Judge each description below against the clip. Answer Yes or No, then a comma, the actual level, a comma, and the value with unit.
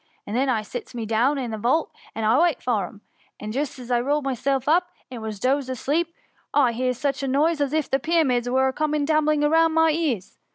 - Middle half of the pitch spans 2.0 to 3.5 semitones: No, average, 3.9 semitones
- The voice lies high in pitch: Yes, very high, 270 Hz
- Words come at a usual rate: No, fast, 230 wpm